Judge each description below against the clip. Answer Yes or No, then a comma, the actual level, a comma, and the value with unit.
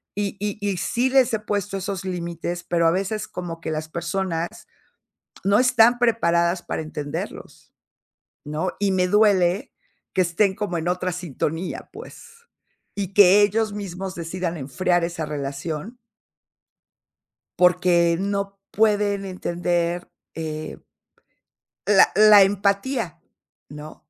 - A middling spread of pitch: Yes, average, 3.1 semitones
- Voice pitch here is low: No, medium, 185 Hz